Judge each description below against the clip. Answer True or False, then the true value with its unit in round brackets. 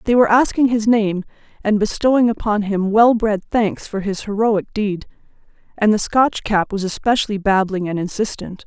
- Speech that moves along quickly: False (165 wpm)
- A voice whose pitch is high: True (210 Hz)